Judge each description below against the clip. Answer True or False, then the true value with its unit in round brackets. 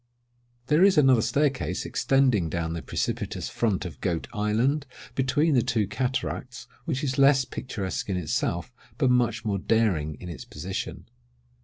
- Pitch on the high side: False (120 Hz)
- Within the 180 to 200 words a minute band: False (150 wpm)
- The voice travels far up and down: True (6.1 semitones)